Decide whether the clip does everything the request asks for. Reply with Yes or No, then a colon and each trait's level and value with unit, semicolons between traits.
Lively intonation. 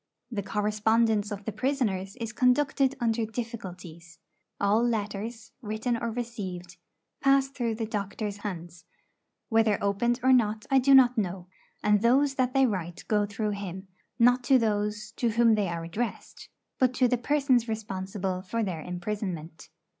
No: average, 3.4 semitones